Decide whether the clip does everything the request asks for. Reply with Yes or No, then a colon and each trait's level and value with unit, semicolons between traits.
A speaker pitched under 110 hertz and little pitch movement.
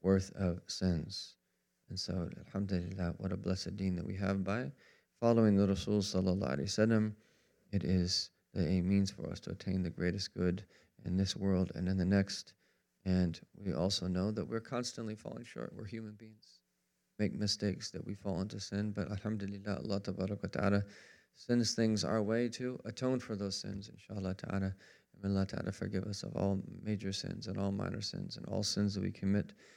Yes: low, 100 Hz; narrow, 2.0 semitones